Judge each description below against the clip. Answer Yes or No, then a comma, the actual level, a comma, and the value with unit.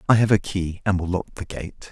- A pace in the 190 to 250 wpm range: No, fast, 280 wpm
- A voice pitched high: No, very low, 95 Hz